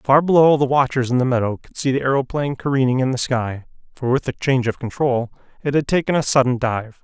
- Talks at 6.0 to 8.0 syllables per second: Yes, 6.1 syllables/s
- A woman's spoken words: No, male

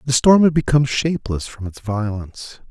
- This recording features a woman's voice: No, male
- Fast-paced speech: No, average, 180 wpm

